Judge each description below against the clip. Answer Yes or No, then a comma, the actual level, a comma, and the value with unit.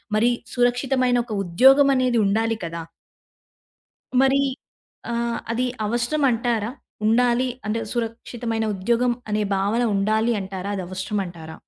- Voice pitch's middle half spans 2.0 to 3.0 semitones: No, average, 3.4 semitones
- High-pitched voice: Yes, high, 230 Hz